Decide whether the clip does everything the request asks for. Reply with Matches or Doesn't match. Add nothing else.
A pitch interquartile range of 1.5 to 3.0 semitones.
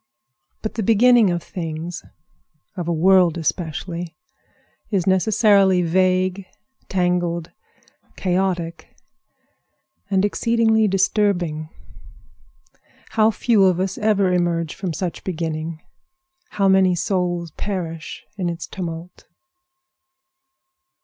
Matches